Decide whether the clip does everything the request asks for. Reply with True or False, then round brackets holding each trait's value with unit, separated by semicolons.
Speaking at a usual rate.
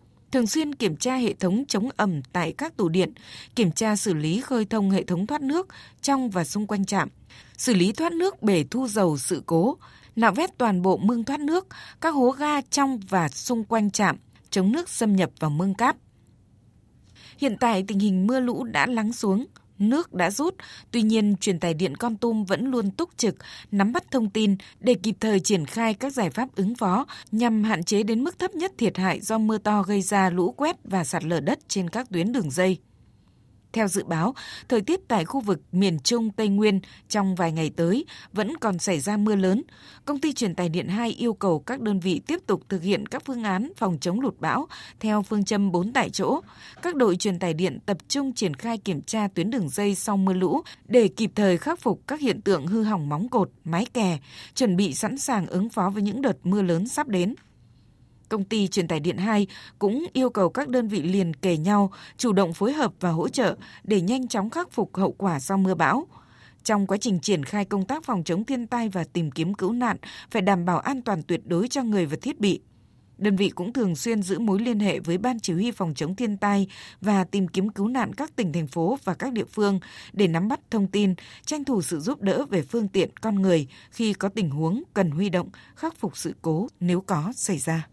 True (230 wpm)